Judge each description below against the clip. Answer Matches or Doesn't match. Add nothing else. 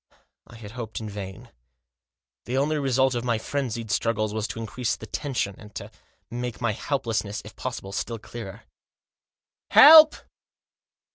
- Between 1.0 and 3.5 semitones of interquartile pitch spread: Matches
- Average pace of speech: Matches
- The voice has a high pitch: Doesn't match